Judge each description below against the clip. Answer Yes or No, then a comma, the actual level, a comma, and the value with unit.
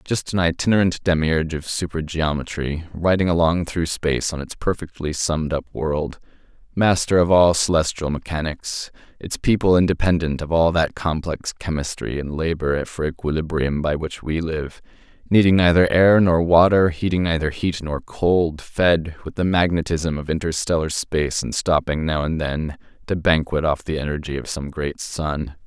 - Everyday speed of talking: Yes, average, 160 wpm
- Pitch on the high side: No, very low, 80 Hz